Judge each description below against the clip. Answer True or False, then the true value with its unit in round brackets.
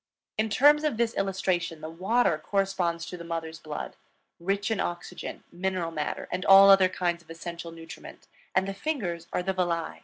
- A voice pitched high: False (180 Hz)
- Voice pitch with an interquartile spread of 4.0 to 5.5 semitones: False (2.7 semitones)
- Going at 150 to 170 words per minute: False (180 wpm)